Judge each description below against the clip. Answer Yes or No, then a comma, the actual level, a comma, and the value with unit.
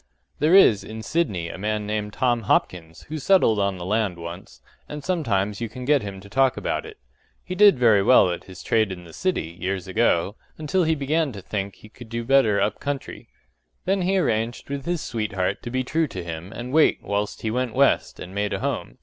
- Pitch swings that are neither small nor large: No, wide, 6.0 semitones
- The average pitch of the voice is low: Yes, low, 110 Hz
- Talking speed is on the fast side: Yes, fast, 220 wpm